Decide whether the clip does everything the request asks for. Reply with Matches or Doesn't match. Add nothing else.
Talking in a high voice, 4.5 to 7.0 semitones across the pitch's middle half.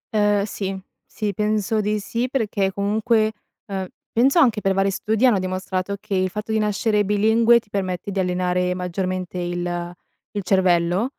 Doesn't match